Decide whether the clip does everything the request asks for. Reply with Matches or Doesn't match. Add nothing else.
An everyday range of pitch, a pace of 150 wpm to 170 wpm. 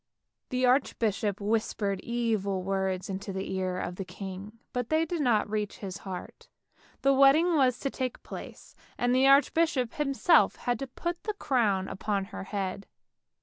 Doesn't match